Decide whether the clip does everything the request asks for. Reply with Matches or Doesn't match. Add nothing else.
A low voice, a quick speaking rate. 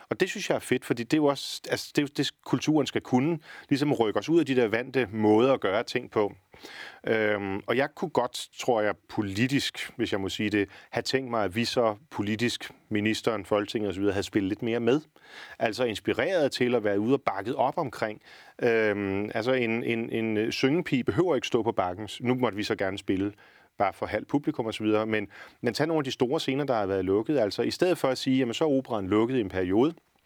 Matches